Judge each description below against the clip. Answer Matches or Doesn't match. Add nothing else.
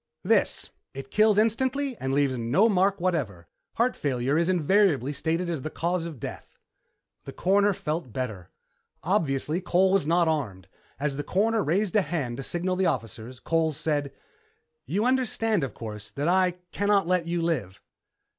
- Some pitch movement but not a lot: Doesn't match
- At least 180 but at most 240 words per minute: Doesn't match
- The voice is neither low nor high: Matches